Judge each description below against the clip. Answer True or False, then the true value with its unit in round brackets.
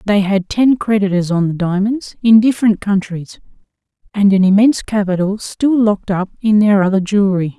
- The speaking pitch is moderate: False (205 Hz)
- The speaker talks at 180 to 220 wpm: False (165 wpm)